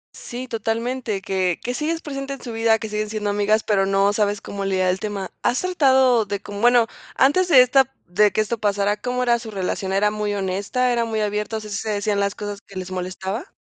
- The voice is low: No, high, 210 Hz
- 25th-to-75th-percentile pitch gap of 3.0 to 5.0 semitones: Yes, average, 3.4 semitones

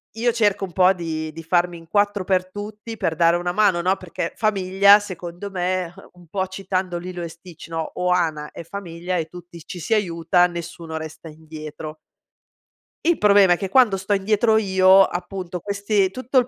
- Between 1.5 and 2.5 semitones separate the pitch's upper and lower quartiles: No, average, 2.9 semitones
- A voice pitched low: No, medium, 185 Hz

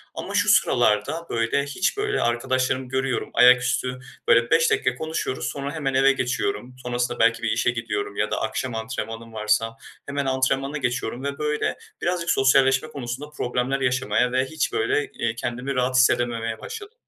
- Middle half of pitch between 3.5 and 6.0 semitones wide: No, average, 3.0 semitones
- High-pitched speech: No, low, 130 Hz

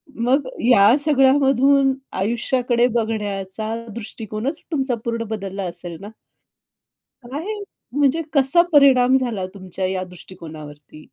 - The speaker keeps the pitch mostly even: No, wide, 5.6 semitones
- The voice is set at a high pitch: Yes, high, 235 Hz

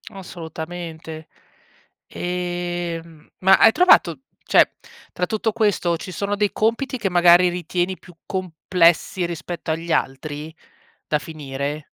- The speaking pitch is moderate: Yes, medium, 175 Hz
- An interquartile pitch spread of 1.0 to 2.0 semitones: No, narrow, 2.6 semitones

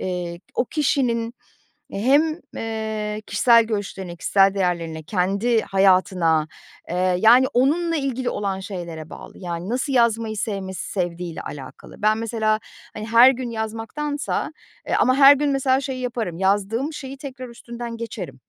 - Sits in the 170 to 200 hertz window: No, high, 220 Hz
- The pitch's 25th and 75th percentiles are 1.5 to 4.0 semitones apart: No, average, 5.0 semitones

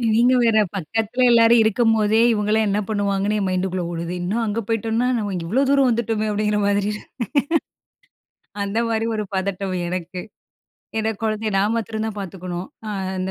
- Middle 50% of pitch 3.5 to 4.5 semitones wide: No, narrow, 2.5 semitones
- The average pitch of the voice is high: Yes, high, 210 Hz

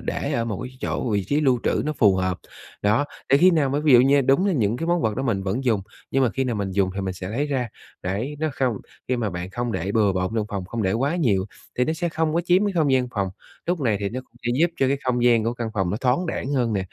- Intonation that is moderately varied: No, wide, 5.7 semitones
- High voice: No, low, 120 Hz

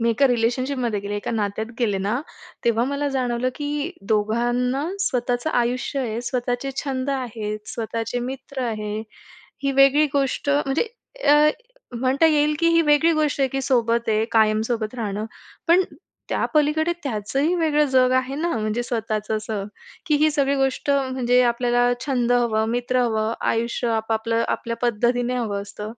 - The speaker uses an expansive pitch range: No, average, 3.5 semitones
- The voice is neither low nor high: No, high, 245 Hz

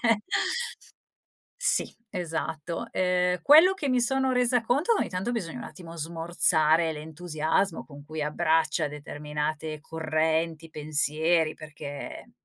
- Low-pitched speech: No, medium, 160 Hz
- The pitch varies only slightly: No, average, 3.1 semitones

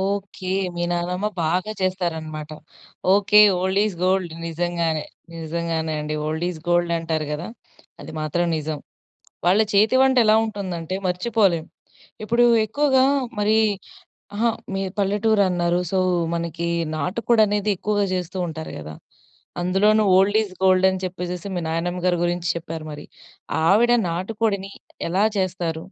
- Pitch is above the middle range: No, medium, 180 Hz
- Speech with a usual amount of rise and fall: Yes, average, 3.4 semitones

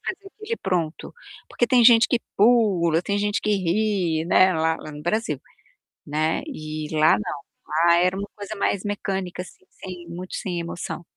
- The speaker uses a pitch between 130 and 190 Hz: Yes, medium, 185 Hz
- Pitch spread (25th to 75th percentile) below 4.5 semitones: Yes, average, 3.9 semitones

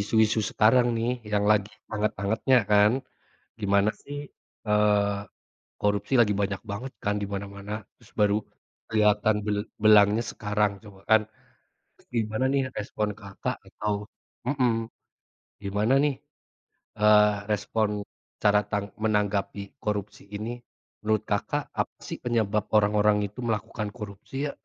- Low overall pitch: Yes, low, 105 Hz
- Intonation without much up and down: Yes, narrow, 1.1 semitones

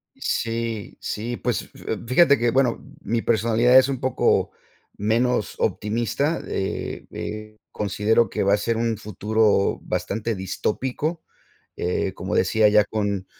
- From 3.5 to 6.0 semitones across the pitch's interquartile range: No, narrow, 2.5 semitones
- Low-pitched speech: Yes, low, 110 Hz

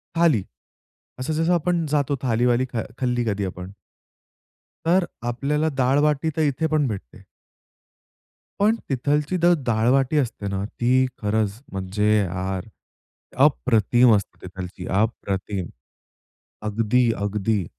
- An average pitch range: No, wide, 6.3 semitones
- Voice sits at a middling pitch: No, low, 120 Hz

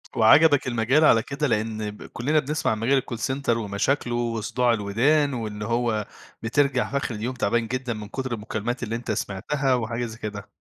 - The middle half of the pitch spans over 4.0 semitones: No, average, 3.3 semitones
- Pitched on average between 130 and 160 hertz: No, low, 120 Hz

